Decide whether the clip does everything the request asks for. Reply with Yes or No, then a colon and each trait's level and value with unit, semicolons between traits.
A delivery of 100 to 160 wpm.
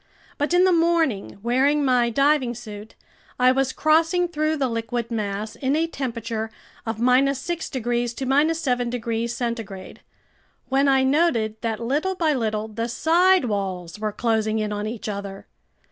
Yes: average, 155 wpm